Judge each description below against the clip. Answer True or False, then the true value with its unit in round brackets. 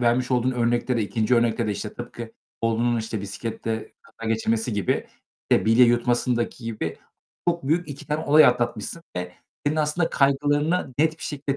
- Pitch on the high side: False (120 Hz)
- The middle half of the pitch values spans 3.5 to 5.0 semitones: True (4.2 semitones)